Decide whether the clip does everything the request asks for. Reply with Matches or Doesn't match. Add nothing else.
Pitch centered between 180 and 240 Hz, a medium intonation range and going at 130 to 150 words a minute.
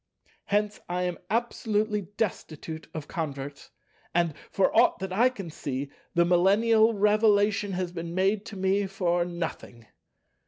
Matches